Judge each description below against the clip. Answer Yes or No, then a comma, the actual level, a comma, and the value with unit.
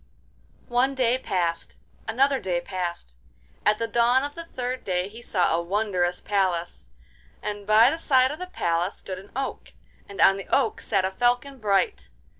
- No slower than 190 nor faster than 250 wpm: No, average, 175 wpm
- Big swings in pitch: Yes, wide, 5.7 semitones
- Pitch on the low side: No, high, 210 Hz